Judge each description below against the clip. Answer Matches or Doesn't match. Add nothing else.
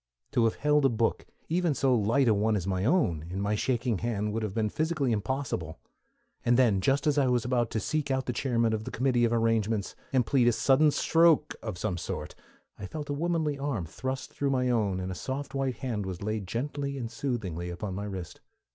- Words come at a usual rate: Doesn't match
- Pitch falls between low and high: Doesn't match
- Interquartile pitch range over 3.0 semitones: Matches